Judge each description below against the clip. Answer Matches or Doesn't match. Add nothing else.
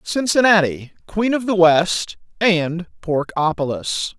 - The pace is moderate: Doesn't match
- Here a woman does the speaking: Doesn't match